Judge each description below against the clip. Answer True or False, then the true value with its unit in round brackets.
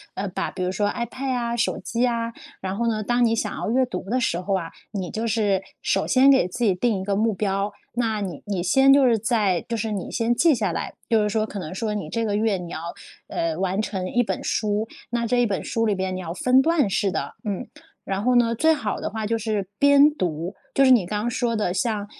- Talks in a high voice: True (215 Hz)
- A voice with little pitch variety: False (3.5 semitones)